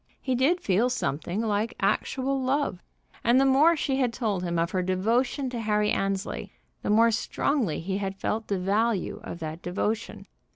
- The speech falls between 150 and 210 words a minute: Yes, average, 175 wpm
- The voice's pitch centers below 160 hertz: No, high, 215 Hz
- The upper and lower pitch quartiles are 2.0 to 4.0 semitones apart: No, average, 5.1 semitones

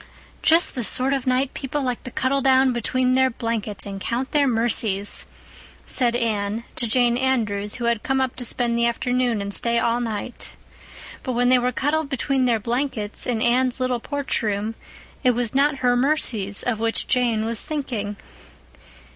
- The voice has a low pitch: No, high, 245 Hz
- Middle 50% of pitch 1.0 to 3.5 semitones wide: Yes, narrow, 2.5 semitones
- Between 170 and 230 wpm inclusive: Yes, average, 180 wpm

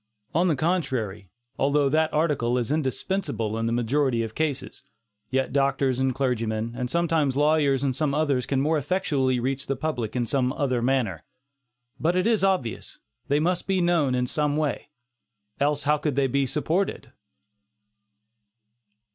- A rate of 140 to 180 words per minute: Yes, average, 155 wpm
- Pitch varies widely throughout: No, average, 3.7 semitones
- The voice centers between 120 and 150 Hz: Yes, medium, 140 Hz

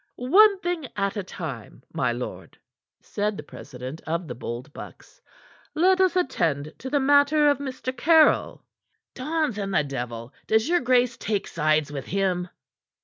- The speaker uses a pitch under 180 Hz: No, high, 215 Hz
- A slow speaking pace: No, average, 155 wpm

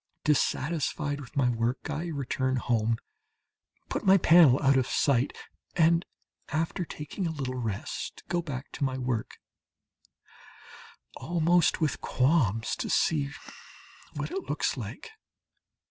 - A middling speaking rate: No, slow, 125 wpm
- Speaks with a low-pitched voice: No, medium, 145 Hz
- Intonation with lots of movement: No, average, 4.4 semitones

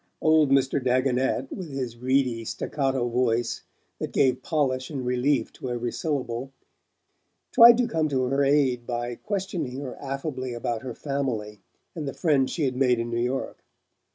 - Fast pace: No, average, 160 wpm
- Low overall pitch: Yes, low, 130 Hz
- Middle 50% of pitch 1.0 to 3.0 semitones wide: Yes, narrow, 2.4 semitones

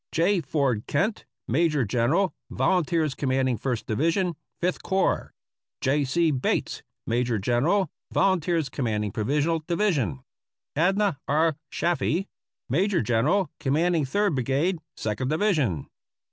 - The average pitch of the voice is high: No, medium, 150 Hz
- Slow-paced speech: Yes, slow, 115 wpm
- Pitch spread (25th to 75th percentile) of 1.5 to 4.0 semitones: No, wide, 5.5 semitones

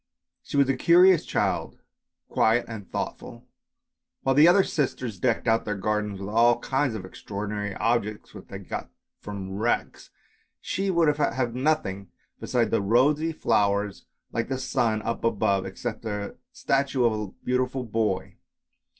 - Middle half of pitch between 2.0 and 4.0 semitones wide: No, average, 4.5 semitones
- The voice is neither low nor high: No, low, 115 Hz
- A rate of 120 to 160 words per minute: Yes, average, 150 wpm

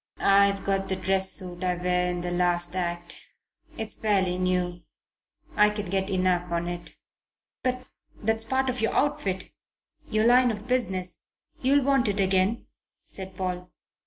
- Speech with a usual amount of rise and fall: Yes, average, 3.5 semitones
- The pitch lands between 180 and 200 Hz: Yes, high, 190 Hz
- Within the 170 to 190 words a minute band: No, average, 155 wpm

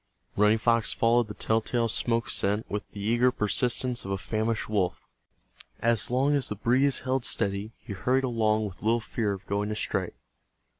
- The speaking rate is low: No, average, 180 wpm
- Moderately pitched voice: No, low, 115 Hz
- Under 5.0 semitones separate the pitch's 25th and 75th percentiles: Yes, narrow, 2.5 semitones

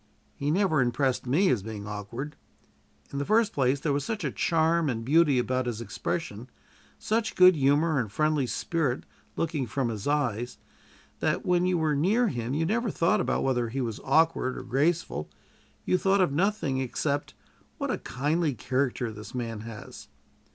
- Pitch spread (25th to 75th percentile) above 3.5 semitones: Yes, average, 5.3 semitones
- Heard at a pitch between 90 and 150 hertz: Yes, medium, 140 Hz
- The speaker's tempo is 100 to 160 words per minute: No, average, 170 wpm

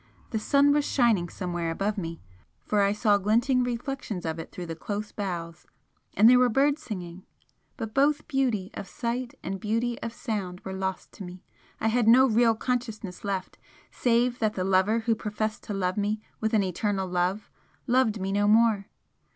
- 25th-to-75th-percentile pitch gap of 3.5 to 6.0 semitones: Yes, average, 3.9 semitones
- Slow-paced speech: No, average, 185 wpm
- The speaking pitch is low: No, high, 215 Hz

